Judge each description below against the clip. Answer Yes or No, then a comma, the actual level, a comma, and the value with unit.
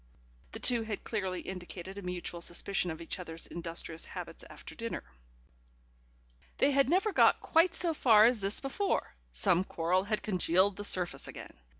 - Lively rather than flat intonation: No, average, 4.8 semitones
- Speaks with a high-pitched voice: Yes, high, 195 Hz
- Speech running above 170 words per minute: No, average, 165 wpm